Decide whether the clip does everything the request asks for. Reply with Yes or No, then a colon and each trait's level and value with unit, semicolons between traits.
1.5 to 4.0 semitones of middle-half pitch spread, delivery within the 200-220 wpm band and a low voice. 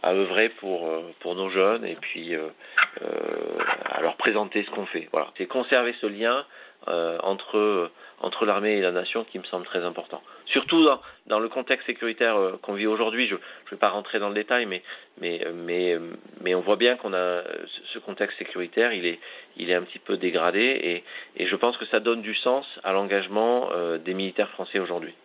No: average, 4.7 semitones; average, 205 wpm; low, 100 Hz